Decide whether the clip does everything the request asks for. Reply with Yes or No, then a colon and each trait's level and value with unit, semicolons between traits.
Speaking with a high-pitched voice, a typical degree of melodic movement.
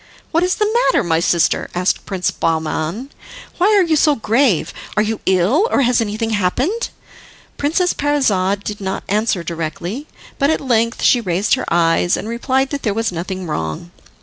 No: high, 220 Hz; wide, 7.5 semitones